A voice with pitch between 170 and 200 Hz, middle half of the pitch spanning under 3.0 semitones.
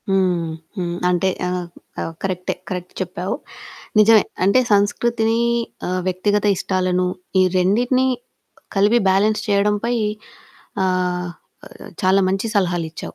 Yes: high, 190 Hz; narrow, 2.4 semitones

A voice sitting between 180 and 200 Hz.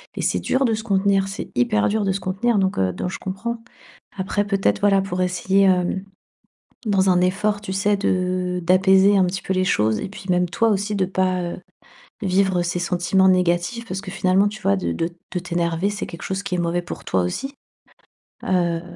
Yes: high, 190 Hz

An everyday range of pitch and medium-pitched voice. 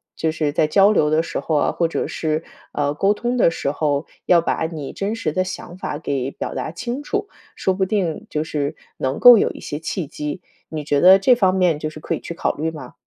Yes: average, 4.2 semitones; medium, 160 Hz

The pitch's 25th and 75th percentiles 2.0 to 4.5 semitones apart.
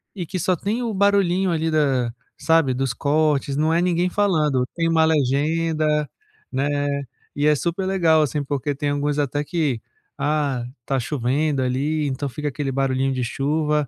Yes: average, 3.0 semitones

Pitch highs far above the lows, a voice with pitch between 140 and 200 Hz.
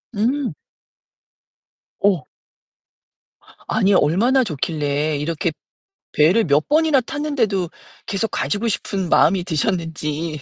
Yes: wide, 6.7 semitones; medium, 185 Hz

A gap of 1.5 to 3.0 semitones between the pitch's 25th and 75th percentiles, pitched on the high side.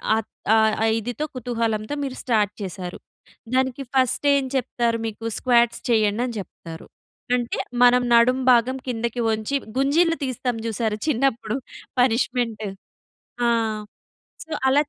Yes: average, 2.7 semitones; high, 235 Hz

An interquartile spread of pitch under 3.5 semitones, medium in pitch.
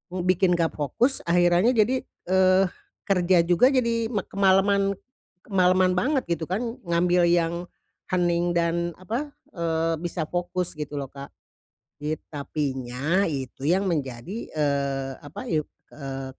No: average, 3.8 semitones; medium, 175 Hz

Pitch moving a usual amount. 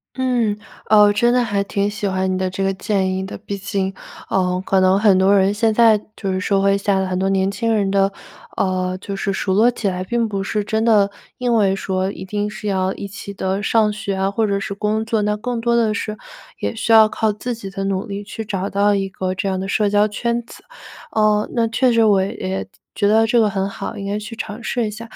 No: narrow, 2.2 semitones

